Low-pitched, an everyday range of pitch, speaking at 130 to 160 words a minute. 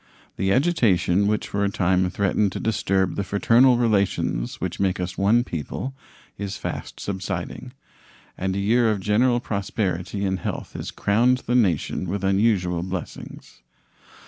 Yes: low, 100 Hz; average, 3.3 semitones; average, 145 wpm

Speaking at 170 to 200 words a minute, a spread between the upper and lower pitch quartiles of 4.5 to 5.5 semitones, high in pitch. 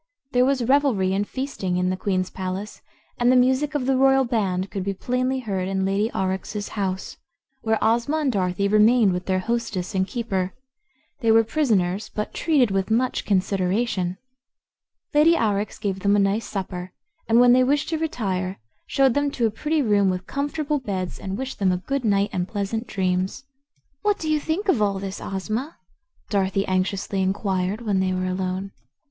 Yes: average, 180 wpm; average, 4.9 semitones; high, 205 Hz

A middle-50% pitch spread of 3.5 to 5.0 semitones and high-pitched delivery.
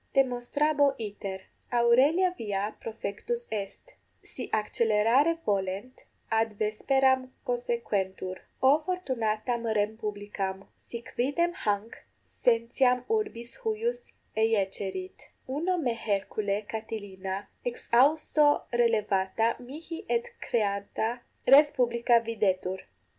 Yes: average, 4.7 semitones; high, 235 Hz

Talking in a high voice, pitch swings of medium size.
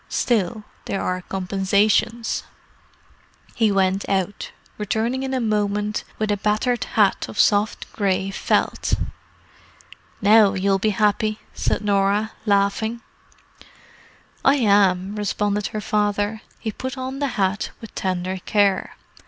No: high, 205 Hz; narrow, 1.9 semitones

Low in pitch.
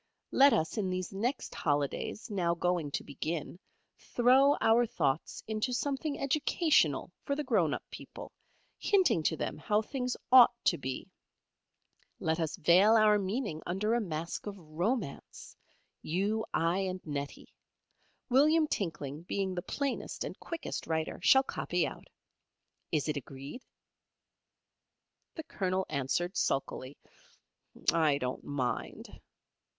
No: medium, 185 Hz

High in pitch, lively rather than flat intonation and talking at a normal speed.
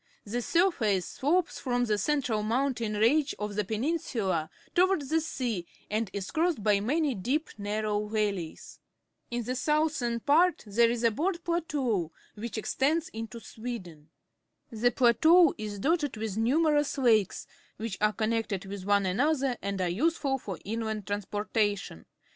Yes: high, 230 Hz; wide, 5.8 semitones; average, 150 wpm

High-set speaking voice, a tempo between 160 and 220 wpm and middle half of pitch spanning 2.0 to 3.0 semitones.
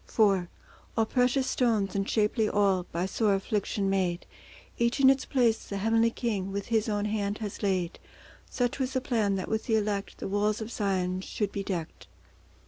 Yes: high, 210 Hz; average, 185 wpm; narrow, 2.6 semitones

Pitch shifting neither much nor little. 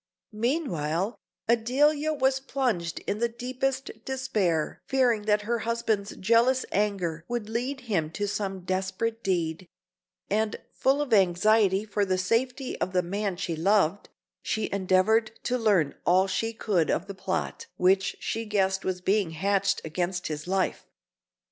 Yes: average, 4.0 semitones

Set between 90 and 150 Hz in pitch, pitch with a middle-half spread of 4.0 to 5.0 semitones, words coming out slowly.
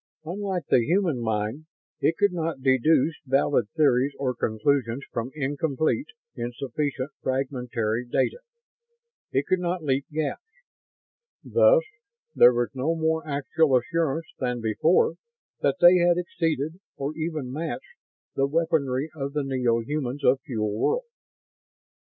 Yes: medium, 140 Hz; average, 4.4 semitones; slow, 125 wpm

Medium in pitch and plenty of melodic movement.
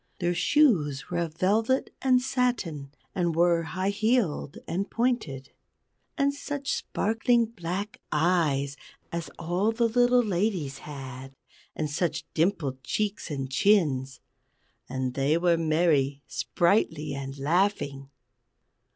Yes: medium, 170 Hz; wide, 7.0 semitones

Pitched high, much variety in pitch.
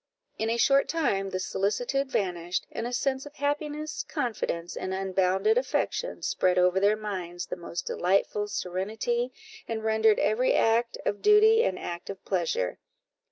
Yes: high, 215 Hz; wide, 6.0 semitones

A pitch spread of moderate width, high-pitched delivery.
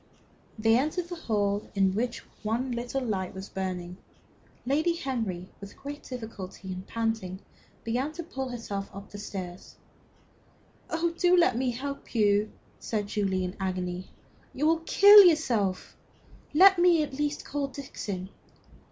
No: wide, 6.9 semitones; high, 230 Hz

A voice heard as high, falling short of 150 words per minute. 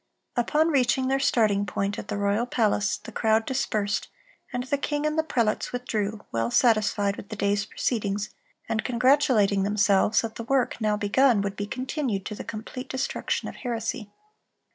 No: high, 220 Hz; average, 170 wpm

